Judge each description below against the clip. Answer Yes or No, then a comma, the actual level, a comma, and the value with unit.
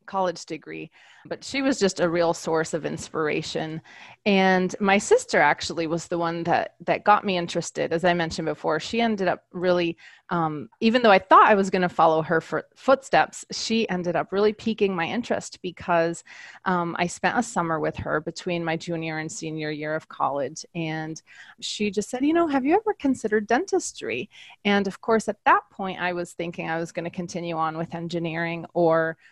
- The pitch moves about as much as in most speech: Yes, average, 3.9 semitones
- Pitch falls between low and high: Yes, medium, 175 Hz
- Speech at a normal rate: Yes, average, 195 wpm